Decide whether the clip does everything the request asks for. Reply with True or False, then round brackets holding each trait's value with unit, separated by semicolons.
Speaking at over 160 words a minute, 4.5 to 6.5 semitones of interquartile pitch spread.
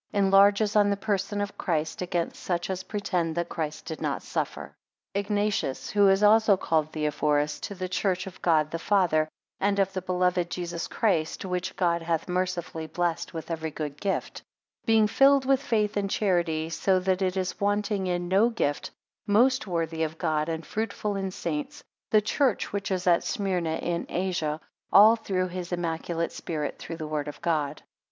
False (175 wpm; 3.7 semitones)